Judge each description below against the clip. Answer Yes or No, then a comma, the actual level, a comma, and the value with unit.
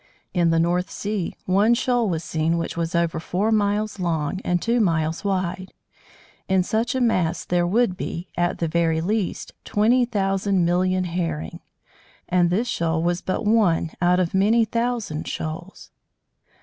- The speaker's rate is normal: Yes, average, 160 wpm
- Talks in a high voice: No, medium, 180 Hz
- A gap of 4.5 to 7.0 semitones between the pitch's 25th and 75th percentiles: No, average, 3.8 semitones